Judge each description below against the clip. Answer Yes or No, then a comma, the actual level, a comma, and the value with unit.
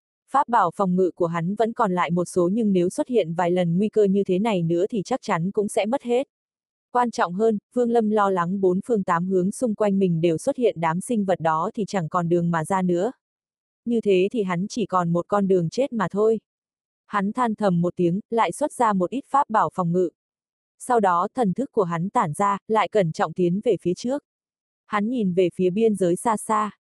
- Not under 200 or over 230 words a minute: No, average, 240 wpm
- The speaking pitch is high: Yes, high, 200 Hz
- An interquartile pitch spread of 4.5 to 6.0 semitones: No, average, 4.1 semitones